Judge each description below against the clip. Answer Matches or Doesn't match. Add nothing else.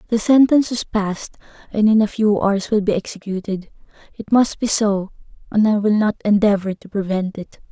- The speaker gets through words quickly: Doesn't match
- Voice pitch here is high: Matches